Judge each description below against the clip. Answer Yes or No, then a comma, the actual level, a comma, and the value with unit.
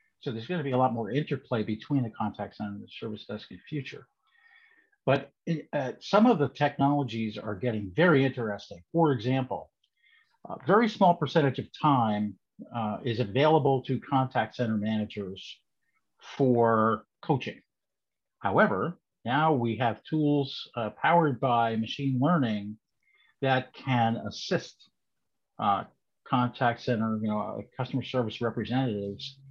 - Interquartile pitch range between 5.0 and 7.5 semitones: No, average, 4.4 semitones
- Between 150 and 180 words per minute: No, average, 140 wpm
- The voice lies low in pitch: Yes, low, 130 Hz